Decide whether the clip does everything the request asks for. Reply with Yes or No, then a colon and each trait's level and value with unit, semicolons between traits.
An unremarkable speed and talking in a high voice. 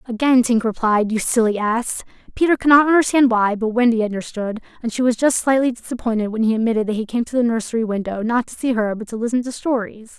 No: fast, 230 wpm; high, 230 Hz